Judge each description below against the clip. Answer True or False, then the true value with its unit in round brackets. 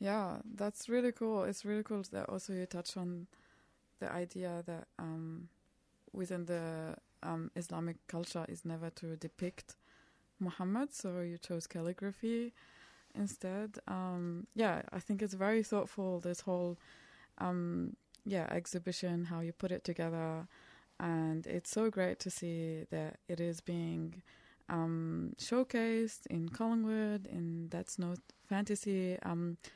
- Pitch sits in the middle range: True (180 Hz)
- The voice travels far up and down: False (3.3 semitones)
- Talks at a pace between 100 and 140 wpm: True (135 wpm)